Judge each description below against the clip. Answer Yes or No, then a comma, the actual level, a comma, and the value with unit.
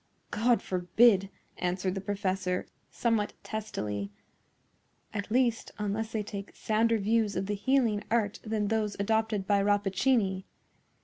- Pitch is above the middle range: Yes, high, 205 Hz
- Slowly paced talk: Yes, slow, 125 wpm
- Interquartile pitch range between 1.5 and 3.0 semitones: Yes, narrow, 2.4 semitones